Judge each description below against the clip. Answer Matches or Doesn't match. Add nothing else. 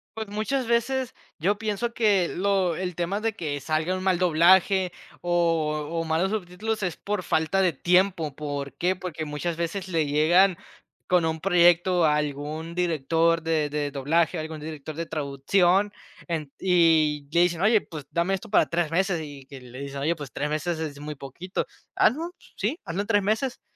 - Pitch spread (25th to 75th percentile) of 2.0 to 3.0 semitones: Doesn't match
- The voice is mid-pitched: Matches